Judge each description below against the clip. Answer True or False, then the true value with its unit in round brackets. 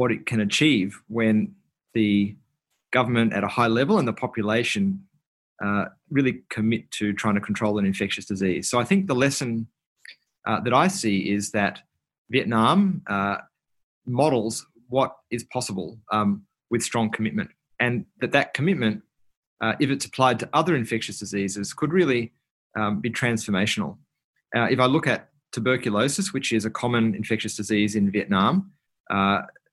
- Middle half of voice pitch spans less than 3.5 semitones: False (3.8 semitones)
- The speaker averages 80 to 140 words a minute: False (155 wpm)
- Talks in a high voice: False (115 Hz)